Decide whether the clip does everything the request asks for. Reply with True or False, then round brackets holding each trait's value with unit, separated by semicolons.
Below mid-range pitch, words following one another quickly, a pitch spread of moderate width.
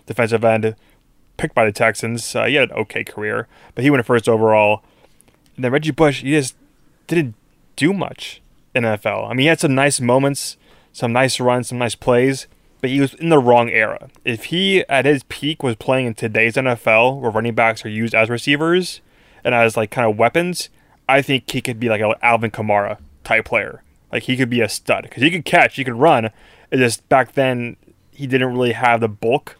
True (125 Hz; 215 wpm; 3.4 semitones)